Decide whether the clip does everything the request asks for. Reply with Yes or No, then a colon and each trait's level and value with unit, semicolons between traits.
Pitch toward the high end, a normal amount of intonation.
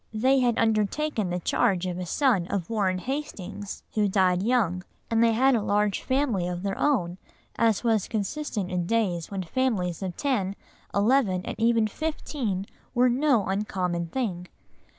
Yes: high, 210 Hz; average, 4.9 semitones